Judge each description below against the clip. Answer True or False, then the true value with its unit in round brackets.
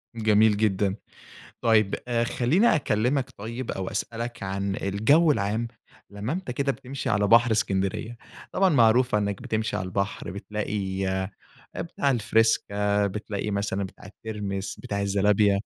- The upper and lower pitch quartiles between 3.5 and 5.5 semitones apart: False (2.9 semitones)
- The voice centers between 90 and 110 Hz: True (105 Hz)